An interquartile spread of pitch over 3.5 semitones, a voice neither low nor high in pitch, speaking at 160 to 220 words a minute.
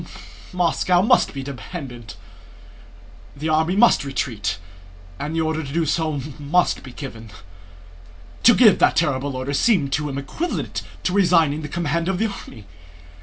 No: average, 4.3 semitones; medium, 155 Hz; average, 150 wpm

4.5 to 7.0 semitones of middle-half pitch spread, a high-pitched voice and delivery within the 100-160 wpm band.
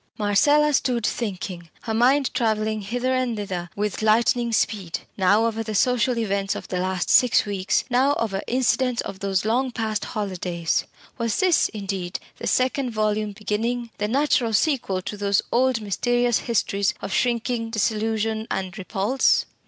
No: average, 3.5 semitones; high, 220 Hz; average, 150 wpm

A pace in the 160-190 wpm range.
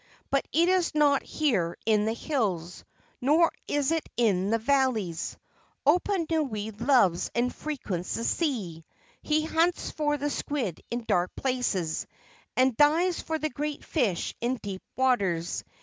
No: average, 140 wpm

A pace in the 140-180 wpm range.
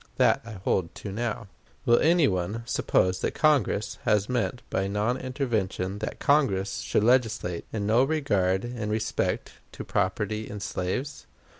Yes: average, 150 wpm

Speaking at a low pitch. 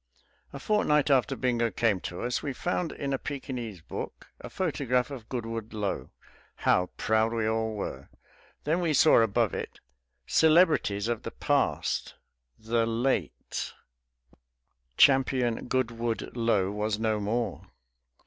Yes: low, 115 Hz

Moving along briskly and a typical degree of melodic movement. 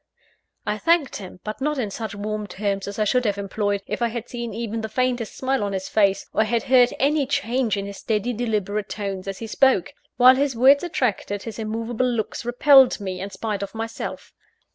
Yes: fast, 210 wpm; average, 3.6 semitones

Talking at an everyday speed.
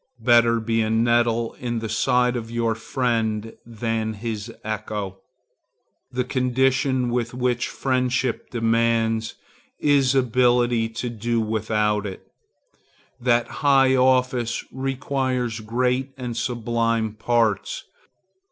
No: slow, 105 wpm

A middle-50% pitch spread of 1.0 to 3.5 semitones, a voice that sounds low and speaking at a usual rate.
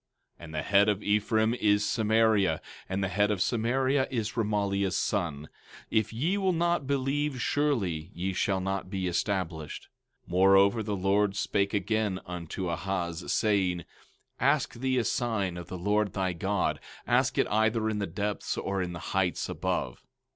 Yes: average, 3.1 semitones; low, 100 Hz; average, 170 wpm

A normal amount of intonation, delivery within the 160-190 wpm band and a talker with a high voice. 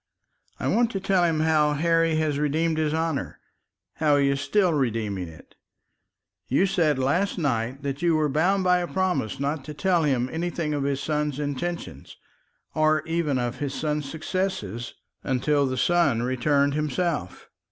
No: average, 3.3 semitones; average, 165 wpm; medium, 150 Hz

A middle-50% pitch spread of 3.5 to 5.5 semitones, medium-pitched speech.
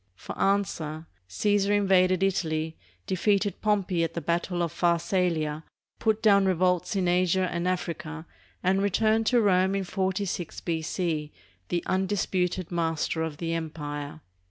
No: average, 3.0 semitones; medium, 180 Hz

